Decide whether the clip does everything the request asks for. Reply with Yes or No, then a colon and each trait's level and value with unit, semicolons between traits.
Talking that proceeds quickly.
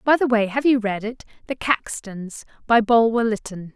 No: average, 175 wpm